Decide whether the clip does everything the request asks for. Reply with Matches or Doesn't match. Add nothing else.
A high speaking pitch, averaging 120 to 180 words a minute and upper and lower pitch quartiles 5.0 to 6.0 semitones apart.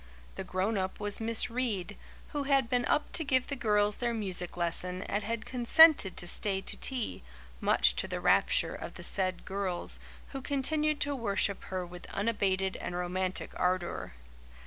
Matches